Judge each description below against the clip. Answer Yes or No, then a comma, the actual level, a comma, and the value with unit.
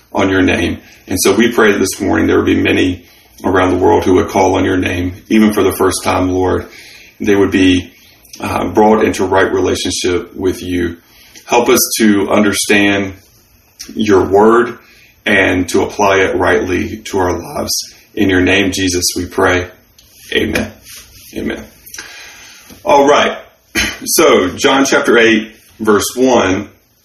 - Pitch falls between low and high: No, very low, 95 Hz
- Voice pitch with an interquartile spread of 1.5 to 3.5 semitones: Yes, narrow, 2.5 semitones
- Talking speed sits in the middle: Yes, average, 150 wpm